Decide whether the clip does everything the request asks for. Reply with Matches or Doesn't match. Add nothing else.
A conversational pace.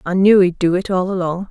Doesn't match